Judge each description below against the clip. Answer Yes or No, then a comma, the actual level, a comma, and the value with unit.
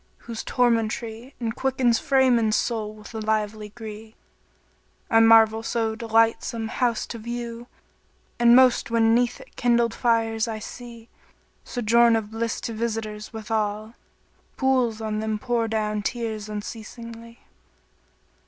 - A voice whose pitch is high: Yes, high, 225 Hz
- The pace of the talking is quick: No, slow, 135 wpm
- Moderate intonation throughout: No, narrow, 1.5 semitones